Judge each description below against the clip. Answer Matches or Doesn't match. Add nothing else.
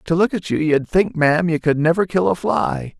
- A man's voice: Matches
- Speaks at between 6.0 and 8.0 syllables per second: Doesn't match